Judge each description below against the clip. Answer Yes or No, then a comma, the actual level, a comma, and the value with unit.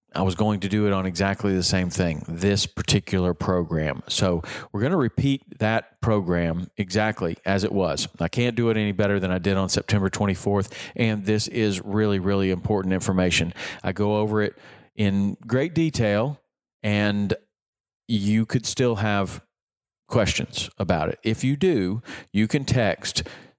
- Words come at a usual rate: Yes, average, 165 wpm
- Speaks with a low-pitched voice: Yes, low, 105 Hz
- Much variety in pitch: No, narrow, 2.5 semitones